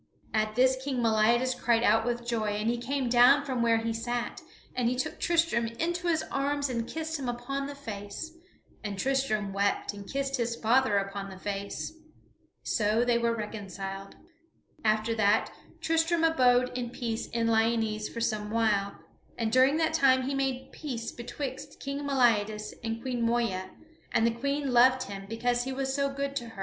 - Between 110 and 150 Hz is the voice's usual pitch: No, high, 240 Hz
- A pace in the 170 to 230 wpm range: Yes, average, 180 wpm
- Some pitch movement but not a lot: Yes, average, 3.5 semitones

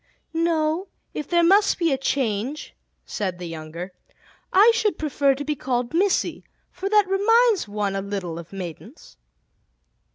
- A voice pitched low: No, very high, 285 Hz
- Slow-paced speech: No, average, 150 wpm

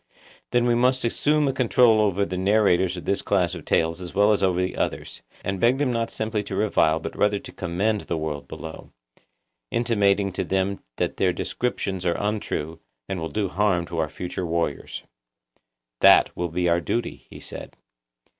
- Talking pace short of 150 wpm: No, average, 185 wpm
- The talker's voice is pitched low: Yes, very low, 95 Hz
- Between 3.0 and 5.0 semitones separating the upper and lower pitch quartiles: Yes, average, 3.8 semitones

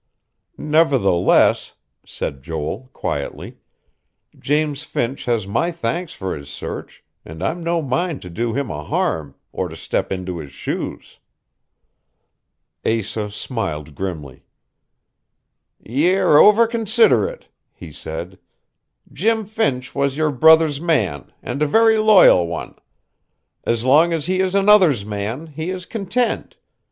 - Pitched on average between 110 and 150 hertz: Yes, medium, 140 Hz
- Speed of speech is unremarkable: No, slow, 125 wpm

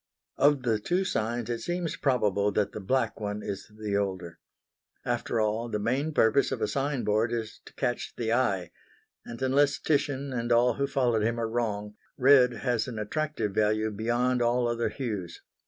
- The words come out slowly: No, average, 180 wpm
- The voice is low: Yes, low, 115 Hz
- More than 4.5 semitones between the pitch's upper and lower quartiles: No, average, 3.4 semitones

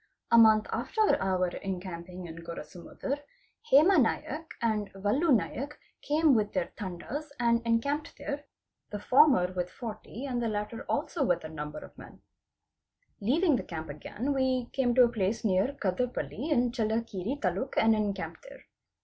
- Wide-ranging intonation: Yes, wide, 6.3 semitones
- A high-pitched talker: Yes, high, 225 Hz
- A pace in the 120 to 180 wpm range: Yes, average, 165 wpm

